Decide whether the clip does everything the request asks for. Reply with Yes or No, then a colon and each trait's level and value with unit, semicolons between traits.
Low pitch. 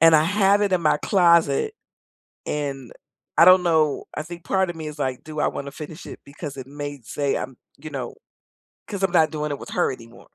No: medium, 155 Hz